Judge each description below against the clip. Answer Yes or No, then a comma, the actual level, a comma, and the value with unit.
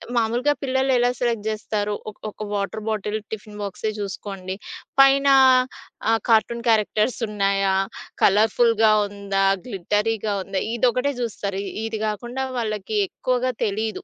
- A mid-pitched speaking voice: No, high, 215 Hz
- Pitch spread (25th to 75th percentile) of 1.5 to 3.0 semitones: Yes, average, 2.7 semitones